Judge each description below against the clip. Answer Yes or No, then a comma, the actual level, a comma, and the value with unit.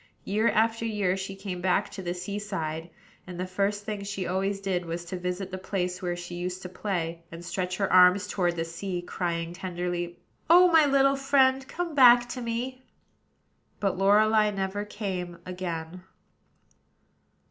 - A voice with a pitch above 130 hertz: Yes, high, 190 Hz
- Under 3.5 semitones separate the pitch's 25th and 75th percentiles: Yes, average, 3.0 semitones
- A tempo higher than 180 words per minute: No, average, 170 wpm